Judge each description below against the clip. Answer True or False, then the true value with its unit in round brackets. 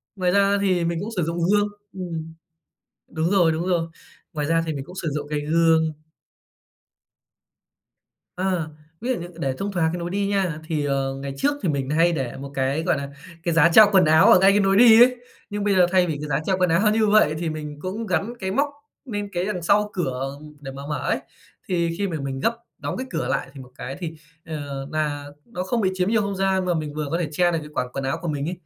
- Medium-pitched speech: True (170 Hz)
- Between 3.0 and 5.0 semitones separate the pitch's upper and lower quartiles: True (4.4 semitones)